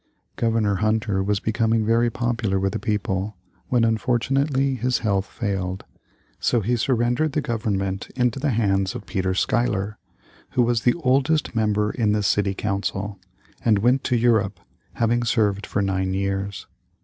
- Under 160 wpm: Yes, average, 150 wpm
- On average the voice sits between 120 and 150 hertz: No, low, 110 Hz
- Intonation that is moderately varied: Yes, average, 3.4 semitones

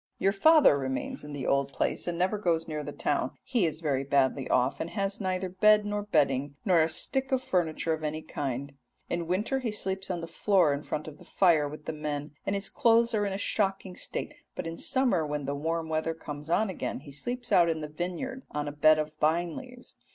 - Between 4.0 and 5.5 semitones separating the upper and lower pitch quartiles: Yes, average, 4.9 semitones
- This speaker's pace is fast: Yes, fast, 230 wpm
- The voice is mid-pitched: Yes, medium, 165 Hz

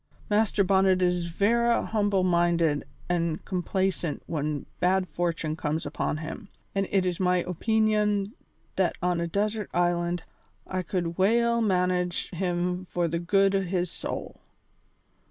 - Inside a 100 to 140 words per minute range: Yes, slow, 135 wpm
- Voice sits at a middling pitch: Yes, medium, 180 Hz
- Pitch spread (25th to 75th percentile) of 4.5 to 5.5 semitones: No, narrow, 2.4 semitones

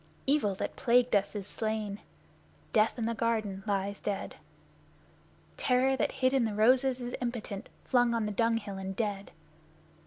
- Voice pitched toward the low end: No, high, 225 Hz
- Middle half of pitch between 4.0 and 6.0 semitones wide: No, average, 3.3 semitones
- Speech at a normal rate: Yes, average, 160 wpm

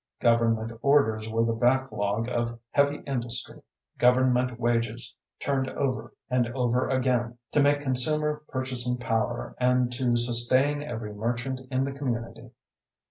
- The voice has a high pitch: No, low, 125 Hz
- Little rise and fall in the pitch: Yes, narrow, 2.1 semitones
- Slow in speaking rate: Yes, slow, 130 wpm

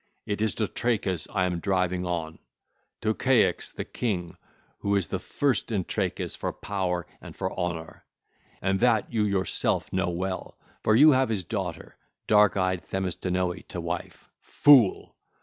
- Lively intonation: No, average, 3.2 semitones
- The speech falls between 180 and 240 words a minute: No, average, 155 wpm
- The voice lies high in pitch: No, very low, 95 Hz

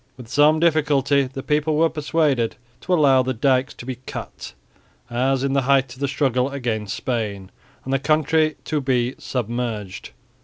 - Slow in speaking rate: No, average, 165 wpm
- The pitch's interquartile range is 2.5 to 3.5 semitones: Yes, average, 3.2 semitones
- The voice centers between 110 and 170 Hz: Yes, low, 135 Hz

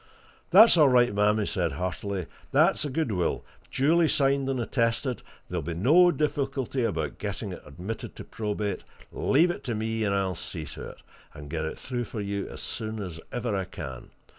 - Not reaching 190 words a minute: No, average, 195 wpm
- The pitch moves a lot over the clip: Yes, wide, 5.9 semitones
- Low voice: Yes, low, 110 Hz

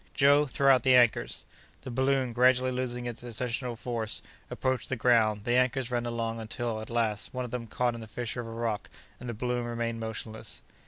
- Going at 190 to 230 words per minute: Yes, fast, 205 wpm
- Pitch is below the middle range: Yes, low, 120 Hz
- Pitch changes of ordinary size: No, narrow, 1.7 semitones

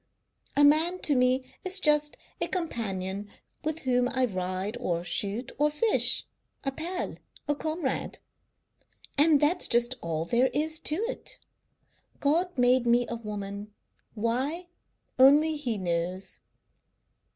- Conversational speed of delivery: No, slow, 130 wpm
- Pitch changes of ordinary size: No, wide, 6.5 semitones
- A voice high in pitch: Yes, very high, 255 Hz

